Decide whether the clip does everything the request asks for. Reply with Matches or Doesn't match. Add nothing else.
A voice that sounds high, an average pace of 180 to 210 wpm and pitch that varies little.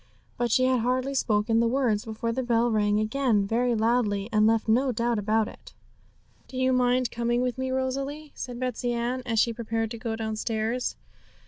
Matches